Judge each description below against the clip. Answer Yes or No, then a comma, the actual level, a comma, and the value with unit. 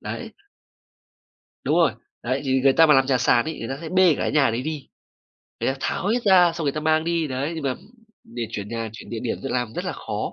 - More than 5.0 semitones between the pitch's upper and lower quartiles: No, average, 4.4 semitones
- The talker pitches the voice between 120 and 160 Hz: Yes, medium, 140 Hz